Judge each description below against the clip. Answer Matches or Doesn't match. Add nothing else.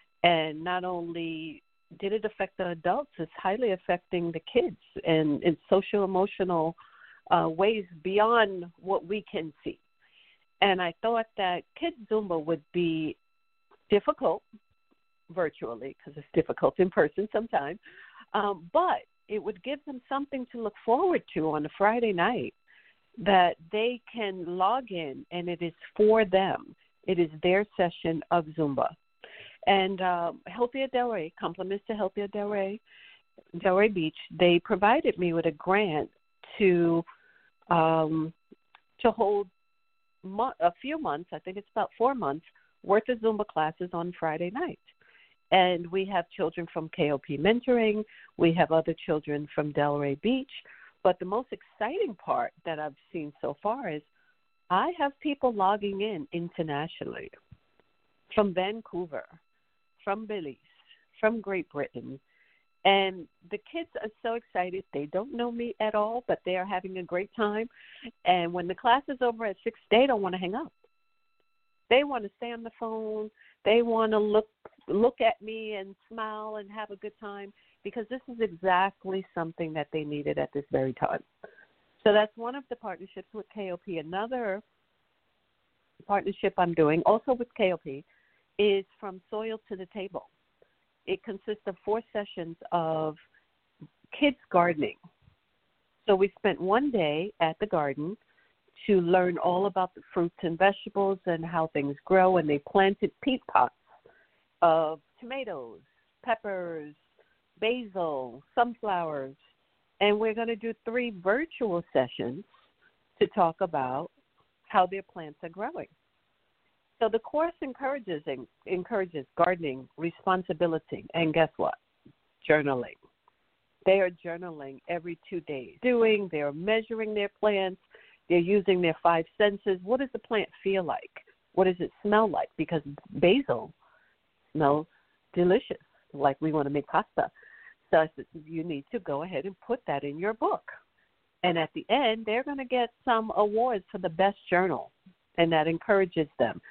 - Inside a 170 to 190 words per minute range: Doesn't match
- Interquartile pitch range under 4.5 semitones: Doesn't match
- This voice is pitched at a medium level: Doesn't match